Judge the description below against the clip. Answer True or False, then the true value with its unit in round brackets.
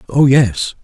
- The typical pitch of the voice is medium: False (130 Hz)